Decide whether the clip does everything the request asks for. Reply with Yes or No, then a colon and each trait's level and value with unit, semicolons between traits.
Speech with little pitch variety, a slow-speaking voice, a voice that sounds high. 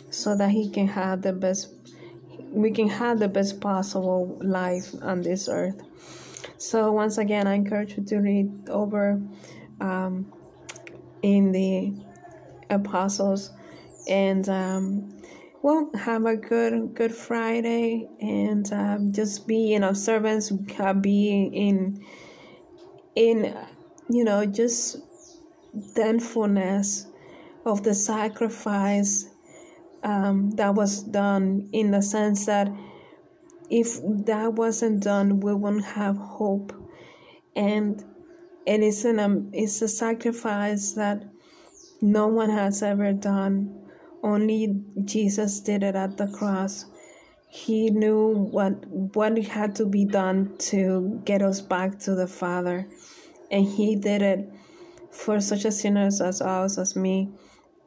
Yes: narrow, 2.2 semitones; slow, 125 wpm; high, 205 Hz